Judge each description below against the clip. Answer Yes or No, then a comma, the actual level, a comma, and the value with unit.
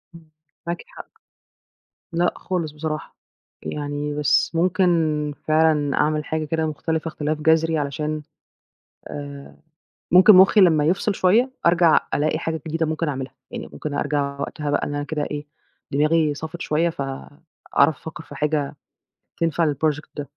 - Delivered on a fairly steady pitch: Yes, narrow, 1.9 semitones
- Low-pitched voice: No, medium, 155 Hz